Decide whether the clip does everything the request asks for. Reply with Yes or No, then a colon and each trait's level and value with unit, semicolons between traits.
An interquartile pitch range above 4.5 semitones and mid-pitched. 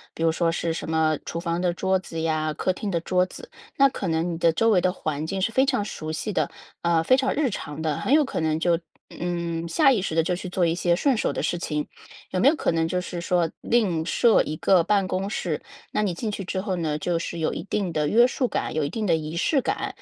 No: average, 3.9 semitones; medium, 175 Hz